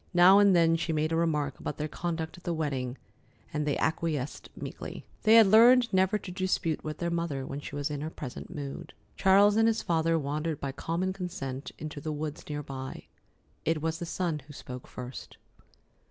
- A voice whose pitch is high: No, medium, 160 Hz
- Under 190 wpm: No, average, 200 wpm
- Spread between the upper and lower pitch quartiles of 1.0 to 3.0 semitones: No, average, 3.5 semitones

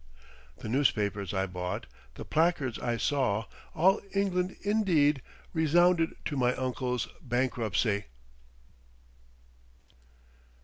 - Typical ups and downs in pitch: No, wide, 7.0 semitones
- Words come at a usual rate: No, slow, 90 wpm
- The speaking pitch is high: No, low, 130 Hz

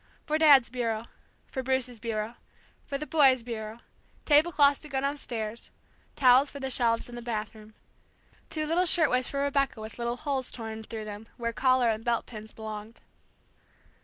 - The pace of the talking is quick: No, average, 165 wpm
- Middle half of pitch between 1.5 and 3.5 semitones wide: No, average, 3.9 semitones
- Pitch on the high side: Yes, high, 245 Hz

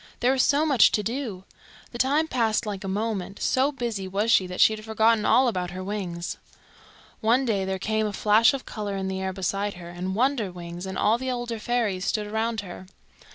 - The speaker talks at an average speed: No, fast, 210 wpm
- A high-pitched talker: Yes, high, 210 Hz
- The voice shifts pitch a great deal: No, average, 3.7 semitones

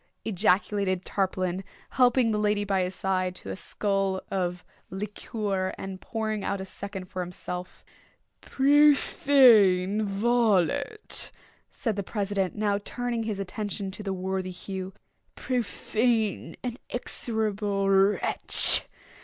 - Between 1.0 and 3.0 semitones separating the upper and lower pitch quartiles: Yes, average, 2.7 semitones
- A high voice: Yes, high, 200 Hz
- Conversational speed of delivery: No, slow, 115 wpm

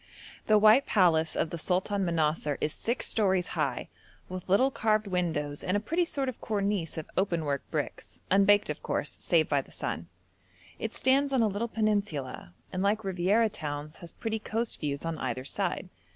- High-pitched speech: Yes, high, 195 Hz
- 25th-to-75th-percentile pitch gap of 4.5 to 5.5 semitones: Yes, average, 5.1 semitones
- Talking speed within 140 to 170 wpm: No, average, 180 wpm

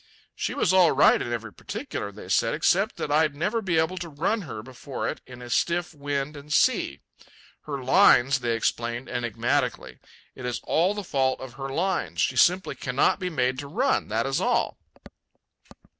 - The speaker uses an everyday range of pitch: No, wide, 5.7 semitones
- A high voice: No, medium, 140 Hz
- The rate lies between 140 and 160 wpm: No, average, 180 wpm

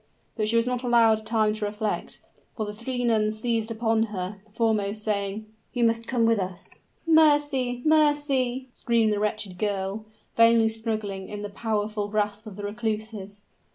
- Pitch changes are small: Yes, narrow, 2.1 semitones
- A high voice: Yes, high, 220 Hz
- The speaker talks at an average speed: Yes, average, 165 wpm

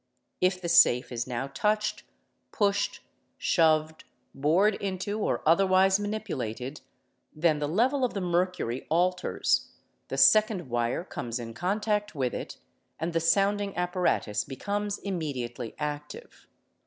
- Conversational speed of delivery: No, slow, 125 wpm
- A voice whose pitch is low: No, medium, 175 Hz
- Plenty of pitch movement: Yes, wide, 6.0 semitones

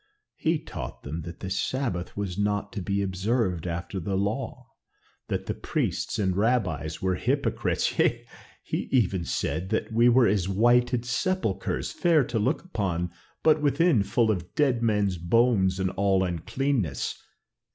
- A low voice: Yes, low, 100 Hz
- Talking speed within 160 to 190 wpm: No, average, 150 wpm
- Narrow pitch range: No, average, 4.8 semitones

